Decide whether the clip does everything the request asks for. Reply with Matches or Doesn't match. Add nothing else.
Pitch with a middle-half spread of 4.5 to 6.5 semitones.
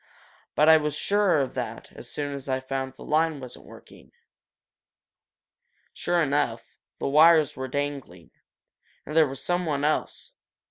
Doesn't match